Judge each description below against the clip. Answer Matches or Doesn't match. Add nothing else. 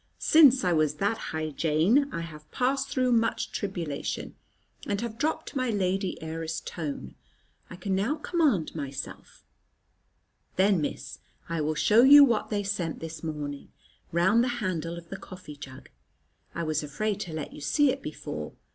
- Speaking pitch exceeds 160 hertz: Matches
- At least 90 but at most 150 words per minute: Doesn't match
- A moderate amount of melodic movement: Doesn't match